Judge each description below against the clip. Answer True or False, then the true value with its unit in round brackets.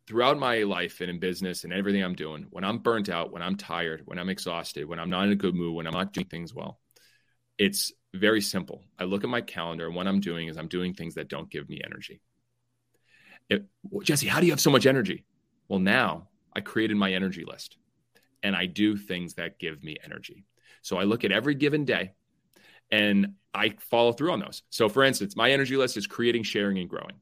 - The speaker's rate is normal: False (225 wpm)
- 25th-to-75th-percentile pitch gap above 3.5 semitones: True (4.8 semitones)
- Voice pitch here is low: True (100 Hz)